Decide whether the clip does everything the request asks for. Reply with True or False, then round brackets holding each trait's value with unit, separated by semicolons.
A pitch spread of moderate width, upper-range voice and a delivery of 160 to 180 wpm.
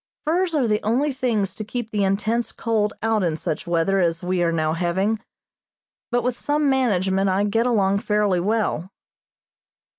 True (4.0 semitones; 210 Hz; 170 wpm)